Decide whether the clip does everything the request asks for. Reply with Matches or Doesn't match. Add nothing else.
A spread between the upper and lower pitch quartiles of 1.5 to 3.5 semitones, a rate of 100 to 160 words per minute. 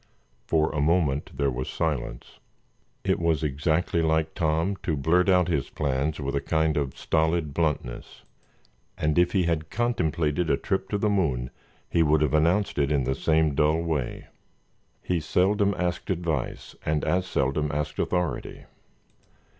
Matches